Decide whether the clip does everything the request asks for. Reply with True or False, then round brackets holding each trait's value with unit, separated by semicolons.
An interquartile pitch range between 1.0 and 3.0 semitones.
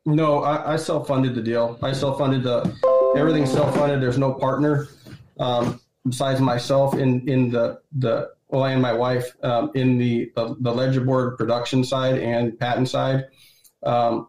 True (2.4 semitones)